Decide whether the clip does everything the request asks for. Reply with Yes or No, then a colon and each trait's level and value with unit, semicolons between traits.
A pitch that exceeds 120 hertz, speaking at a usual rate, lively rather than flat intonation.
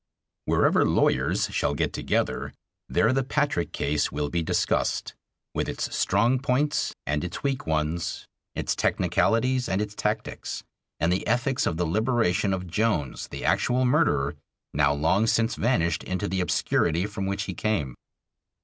No: low, 100 Hz; average, 150 wpm; wide, 6.4 semitones